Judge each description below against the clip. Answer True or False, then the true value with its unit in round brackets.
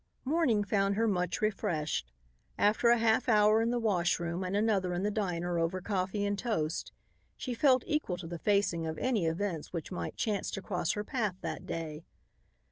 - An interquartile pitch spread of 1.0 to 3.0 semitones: False (4.2 semitones)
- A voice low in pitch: False (200 Hz)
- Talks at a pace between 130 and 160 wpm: False (185 wpm)